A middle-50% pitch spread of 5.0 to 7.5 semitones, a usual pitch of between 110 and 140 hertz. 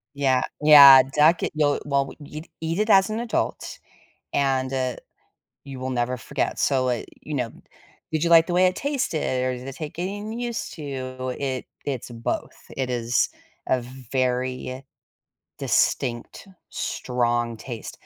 No: average, 3.7 semitones; low, 135 Hz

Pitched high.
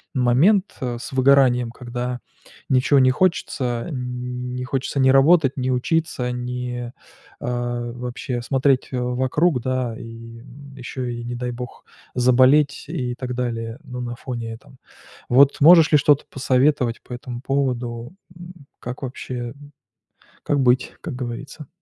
No: low, 125 Hz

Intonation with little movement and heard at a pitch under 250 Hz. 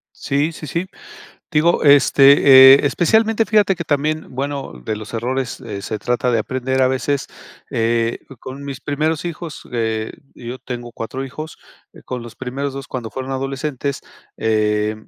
No: average, 3.5 semitones; low, 135 Hz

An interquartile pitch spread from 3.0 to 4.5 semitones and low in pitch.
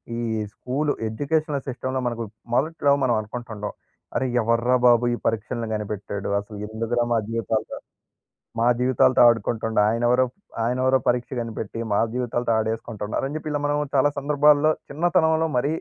Yes: average, 3.7 semitones; low, 120 Hz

